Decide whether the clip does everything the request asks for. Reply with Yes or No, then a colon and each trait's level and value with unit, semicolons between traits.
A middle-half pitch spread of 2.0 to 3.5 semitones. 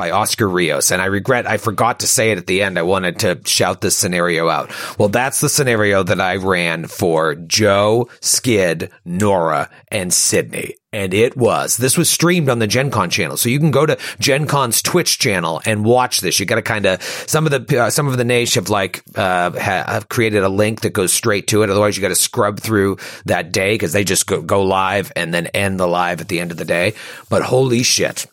No: average, 4.7 semitones